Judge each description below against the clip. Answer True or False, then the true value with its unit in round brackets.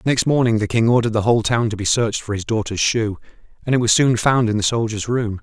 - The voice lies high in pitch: False (110 Hz)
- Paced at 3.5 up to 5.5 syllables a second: False (6.4 syllables/s)